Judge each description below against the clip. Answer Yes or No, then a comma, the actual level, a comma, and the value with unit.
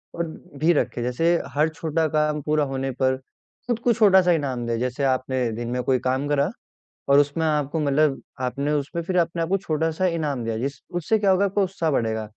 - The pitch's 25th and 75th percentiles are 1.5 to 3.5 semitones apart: No, average, 4.1 semitones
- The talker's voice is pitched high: No, medium, 150 Hz